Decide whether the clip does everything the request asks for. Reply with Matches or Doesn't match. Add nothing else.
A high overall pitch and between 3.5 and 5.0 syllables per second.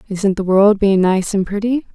Matches